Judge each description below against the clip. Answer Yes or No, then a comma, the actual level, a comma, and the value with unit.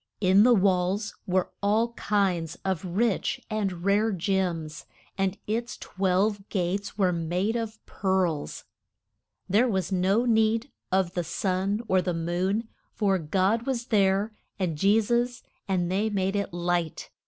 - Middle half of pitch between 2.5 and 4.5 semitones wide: Yes, average, 3.0 semitones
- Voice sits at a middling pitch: No, high, 195 Hz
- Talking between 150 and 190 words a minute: No, average, 140 wpm